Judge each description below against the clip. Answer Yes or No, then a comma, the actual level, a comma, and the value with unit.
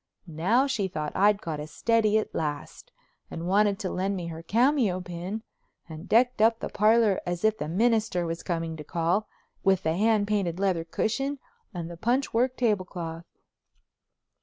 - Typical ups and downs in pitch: Yes, average, 4.7 semitones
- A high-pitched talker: Yes, high, 195 Hz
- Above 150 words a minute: Yes, average, 170 wpm